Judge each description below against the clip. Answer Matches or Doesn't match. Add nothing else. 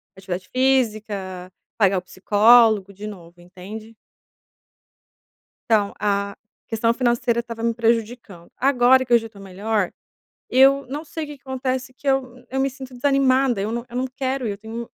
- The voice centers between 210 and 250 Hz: Matches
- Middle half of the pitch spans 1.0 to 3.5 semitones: Doesn't match